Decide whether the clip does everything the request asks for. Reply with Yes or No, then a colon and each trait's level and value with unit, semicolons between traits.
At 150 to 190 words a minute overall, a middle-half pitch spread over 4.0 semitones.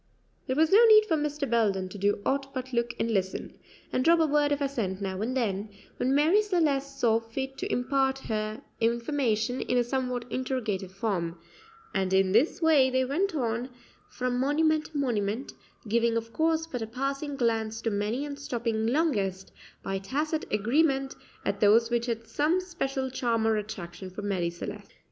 Yes: average, 180 wpm; average, 4.6 semitones